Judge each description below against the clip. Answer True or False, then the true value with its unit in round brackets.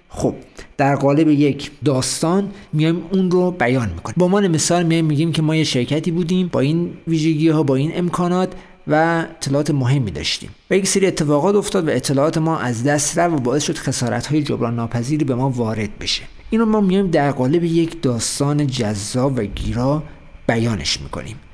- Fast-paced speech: True (180 wpm)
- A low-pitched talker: False (150 Hz)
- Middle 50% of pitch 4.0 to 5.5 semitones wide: True (4.9 semitones)